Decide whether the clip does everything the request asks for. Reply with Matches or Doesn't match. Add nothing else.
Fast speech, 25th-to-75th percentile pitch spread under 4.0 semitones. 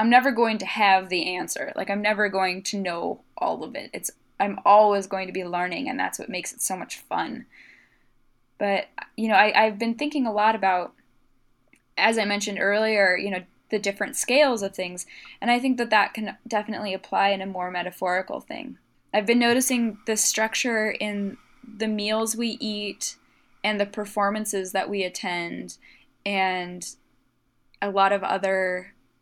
Doesn't match